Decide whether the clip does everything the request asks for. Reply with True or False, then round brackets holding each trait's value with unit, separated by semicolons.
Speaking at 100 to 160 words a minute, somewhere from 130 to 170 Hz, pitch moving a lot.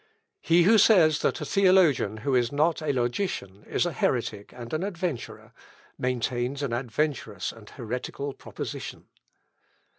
True (140 wpm; 135 Hz; 5.9 semitones)